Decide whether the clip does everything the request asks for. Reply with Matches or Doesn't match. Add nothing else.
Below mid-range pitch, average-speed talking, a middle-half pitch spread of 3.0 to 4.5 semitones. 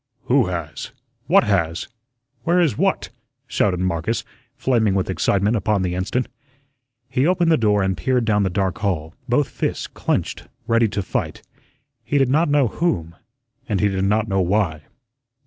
Doesn't match